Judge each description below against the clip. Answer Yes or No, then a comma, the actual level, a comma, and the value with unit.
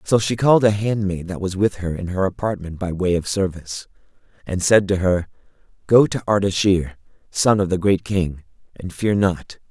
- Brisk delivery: No, average, 190 wpm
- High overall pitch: No, very low, 95 Hz